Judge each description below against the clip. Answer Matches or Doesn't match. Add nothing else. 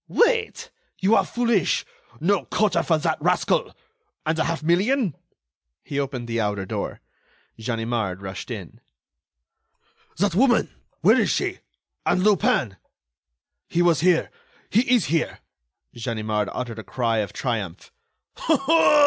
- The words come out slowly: Matches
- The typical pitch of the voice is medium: Matches